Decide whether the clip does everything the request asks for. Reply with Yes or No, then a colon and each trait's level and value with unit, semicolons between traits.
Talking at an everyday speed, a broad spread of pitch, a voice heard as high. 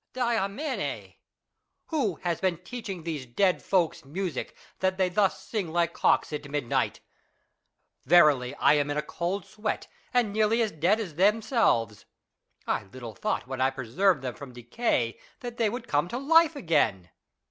No: average, 160 wpm; wide, 7.0 semitones; medium, 175 Hz